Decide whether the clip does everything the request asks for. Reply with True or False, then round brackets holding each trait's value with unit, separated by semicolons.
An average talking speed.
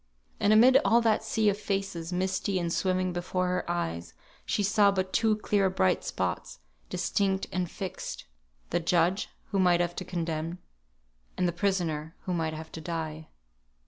True (165 wpm)